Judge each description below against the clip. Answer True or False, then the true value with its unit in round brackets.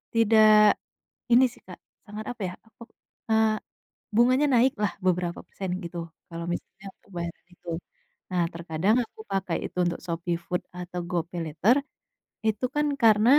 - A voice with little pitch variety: False (4.1 semitones)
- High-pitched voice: True (195 Hz)